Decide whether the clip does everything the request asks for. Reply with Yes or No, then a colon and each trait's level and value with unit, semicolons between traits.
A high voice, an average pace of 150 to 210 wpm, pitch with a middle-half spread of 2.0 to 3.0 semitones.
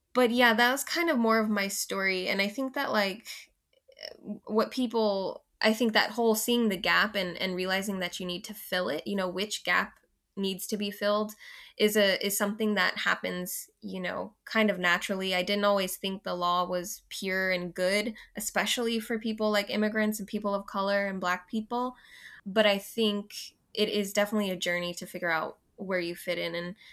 Yes: high, 205 Hz; average, 200 wpm; narrow, 2.6 semitones